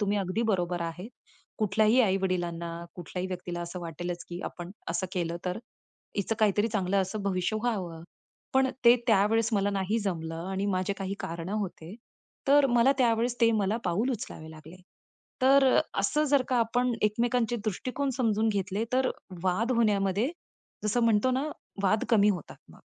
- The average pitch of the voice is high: Yes, high, 200 Hz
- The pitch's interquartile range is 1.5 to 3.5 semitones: No, average, 4.1 semitones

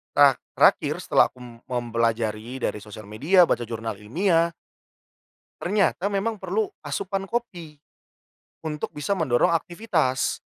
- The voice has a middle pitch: Yes, medium, 150 Hz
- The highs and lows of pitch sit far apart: Yes, wide, 8.6 semitones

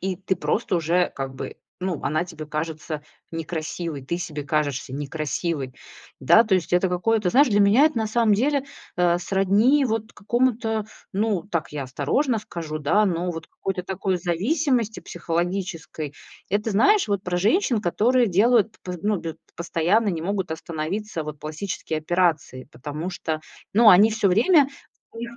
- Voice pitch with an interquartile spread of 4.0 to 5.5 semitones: Yes, average, 5.2 semitones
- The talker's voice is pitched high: No, medium, 180 Hz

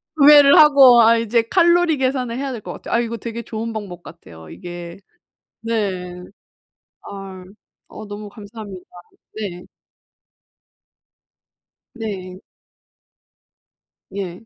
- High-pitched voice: Yes, high, 220 Hz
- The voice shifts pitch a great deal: No, average, 4.4 semitones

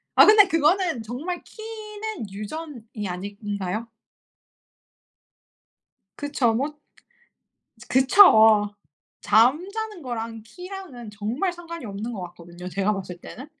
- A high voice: Yes, high, 240 Hz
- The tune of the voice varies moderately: No, wide, 9.0 semitones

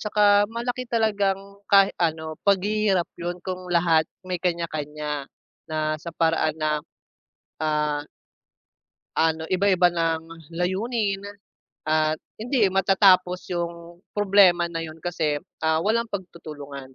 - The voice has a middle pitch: Yes, medium, 175 Hz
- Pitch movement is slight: No, average, 3.8 semitones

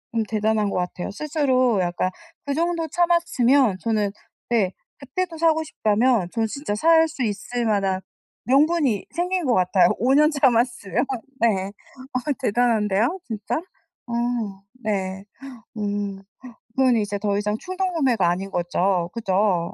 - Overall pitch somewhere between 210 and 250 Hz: Yes, high, 230 Hz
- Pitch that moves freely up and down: Yes, wide, 6.1 semitones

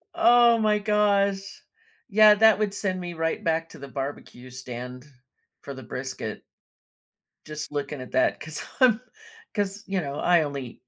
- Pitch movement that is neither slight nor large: No, wide, 6.9 semitones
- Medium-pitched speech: Yes, medium, 175 Hz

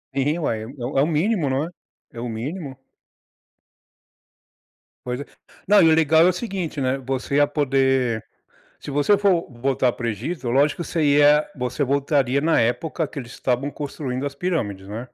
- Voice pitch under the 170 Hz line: Yes, medium, 140 Hz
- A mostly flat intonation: No, average, 3.8 semitones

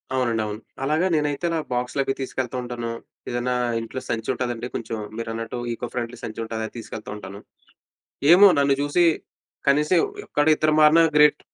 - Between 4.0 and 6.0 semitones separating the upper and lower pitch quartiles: Yes, average, 4.3 semitones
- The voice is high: No, low, 125 Hz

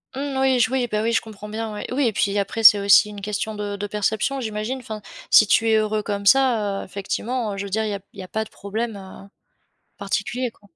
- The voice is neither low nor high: No, high, 215 Hz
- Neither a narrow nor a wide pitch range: No, narrow, 2.2 semitones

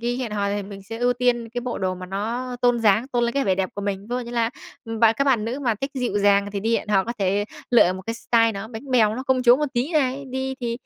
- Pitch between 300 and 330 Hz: No, high, 230 Hz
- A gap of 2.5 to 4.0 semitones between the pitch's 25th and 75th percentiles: Yes, average, 3.5 semitones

